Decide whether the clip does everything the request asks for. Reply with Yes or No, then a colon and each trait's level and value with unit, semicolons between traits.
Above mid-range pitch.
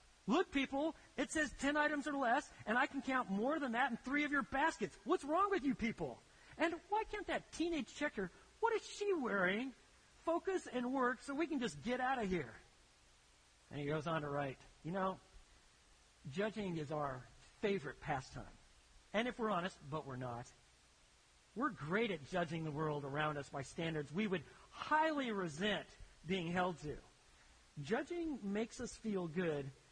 Yes: high, 205 Hz